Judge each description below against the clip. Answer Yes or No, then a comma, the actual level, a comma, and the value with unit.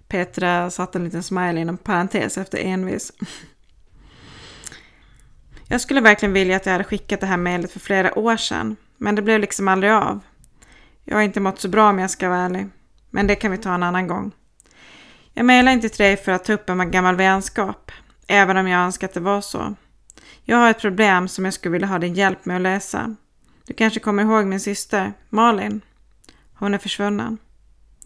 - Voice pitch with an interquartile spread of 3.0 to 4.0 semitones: No, narrow, 2.5 semitones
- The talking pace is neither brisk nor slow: No, fast, 200 wpm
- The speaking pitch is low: No, high, 195 Hz